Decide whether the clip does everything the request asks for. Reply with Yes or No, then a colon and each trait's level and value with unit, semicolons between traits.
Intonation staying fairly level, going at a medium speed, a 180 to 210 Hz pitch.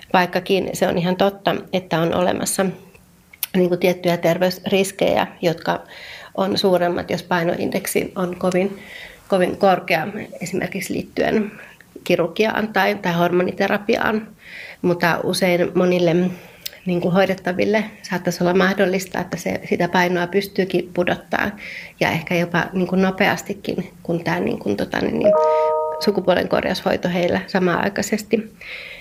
Yes: narrow, 1.9 semitones; average, 120 wpm; medium, 185 Hz